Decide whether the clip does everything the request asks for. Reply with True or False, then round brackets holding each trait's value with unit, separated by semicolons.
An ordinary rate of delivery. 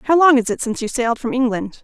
False (295 wpm)